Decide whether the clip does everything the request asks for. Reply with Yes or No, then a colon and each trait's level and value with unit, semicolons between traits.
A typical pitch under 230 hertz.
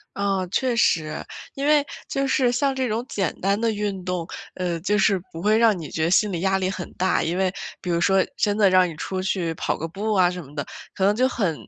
Yes: high, 195 Hz